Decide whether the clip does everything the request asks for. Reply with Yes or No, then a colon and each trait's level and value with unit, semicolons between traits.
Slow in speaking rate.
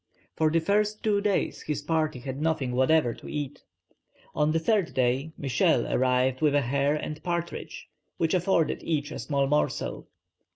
No: average, 165 wpm